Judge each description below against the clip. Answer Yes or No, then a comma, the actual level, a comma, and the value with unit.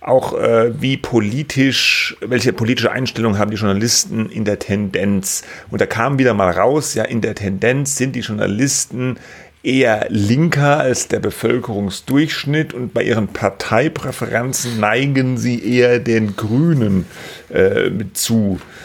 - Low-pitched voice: Yes, low, 120 Hz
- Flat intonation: No, average, 3.3 semitones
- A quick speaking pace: No, average, 135 wpm